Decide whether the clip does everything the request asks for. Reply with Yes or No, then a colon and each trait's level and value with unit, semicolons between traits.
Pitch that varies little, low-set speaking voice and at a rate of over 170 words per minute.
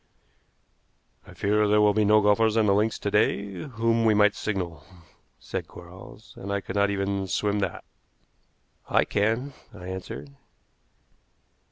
No: narrow, 1.6 semitones; low, 105 Hz; average, 155 wpm